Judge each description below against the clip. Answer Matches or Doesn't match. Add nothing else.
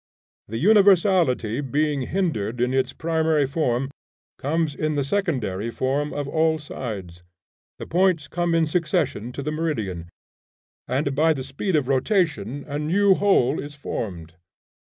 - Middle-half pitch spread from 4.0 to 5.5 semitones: Matches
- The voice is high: Doesn't match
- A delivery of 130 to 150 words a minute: Matches